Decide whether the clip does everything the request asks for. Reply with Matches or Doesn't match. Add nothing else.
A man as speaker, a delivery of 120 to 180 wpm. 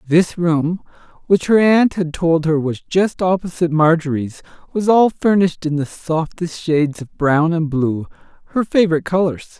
Matches